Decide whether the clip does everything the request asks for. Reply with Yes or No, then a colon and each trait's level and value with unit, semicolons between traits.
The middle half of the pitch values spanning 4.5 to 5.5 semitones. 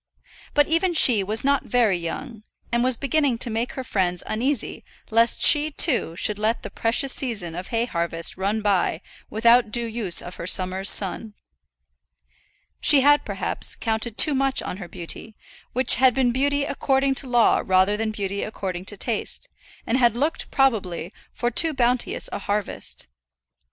Yes: average, 4.9 semitones